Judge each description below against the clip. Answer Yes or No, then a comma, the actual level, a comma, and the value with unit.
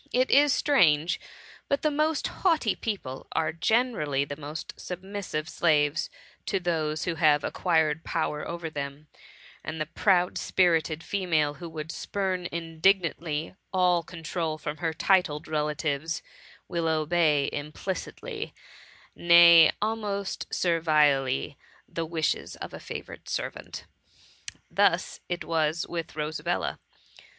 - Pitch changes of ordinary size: Yes, average, 3.1 semitones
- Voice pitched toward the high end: No, medium, 165 Hz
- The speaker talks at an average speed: No, slow, 120 wpm